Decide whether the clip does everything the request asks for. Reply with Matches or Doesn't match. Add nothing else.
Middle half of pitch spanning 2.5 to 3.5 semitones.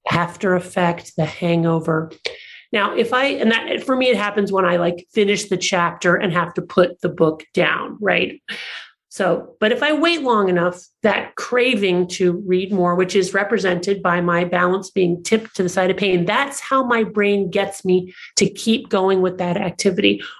Matches